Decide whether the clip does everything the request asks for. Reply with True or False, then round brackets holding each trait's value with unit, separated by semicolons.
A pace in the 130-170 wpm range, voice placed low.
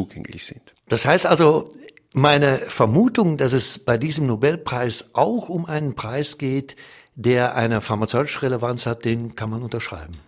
True (140 wpm; 130 Hz)